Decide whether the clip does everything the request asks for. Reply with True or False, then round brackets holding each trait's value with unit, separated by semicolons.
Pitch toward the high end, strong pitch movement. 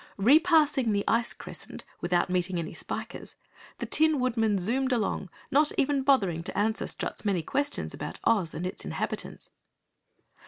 True (225 Hz; 6.7 semitones)